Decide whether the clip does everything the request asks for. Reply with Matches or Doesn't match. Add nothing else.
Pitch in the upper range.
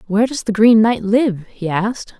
Matches